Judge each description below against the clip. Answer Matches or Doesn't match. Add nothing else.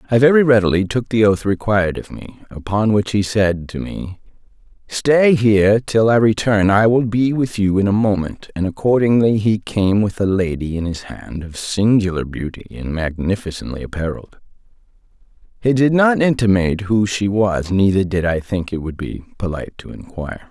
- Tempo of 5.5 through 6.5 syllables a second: Doesn't match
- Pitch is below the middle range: Matches